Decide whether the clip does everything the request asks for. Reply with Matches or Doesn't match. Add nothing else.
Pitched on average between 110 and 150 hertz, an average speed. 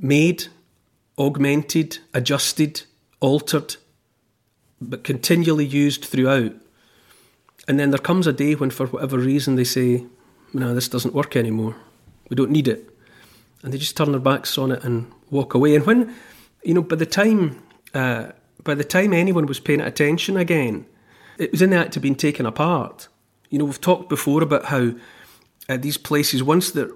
Matches